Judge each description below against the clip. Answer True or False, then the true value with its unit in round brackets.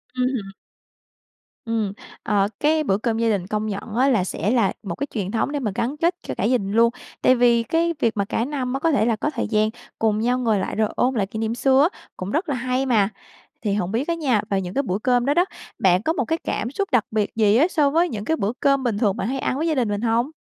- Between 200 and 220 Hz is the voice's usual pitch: False (235 Hz)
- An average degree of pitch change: True (4.5 semitones)